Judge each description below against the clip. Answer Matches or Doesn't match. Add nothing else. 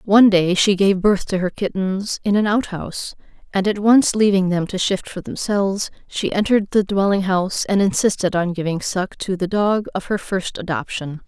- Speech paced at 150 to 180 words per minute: Doesn't match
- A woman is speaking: Matches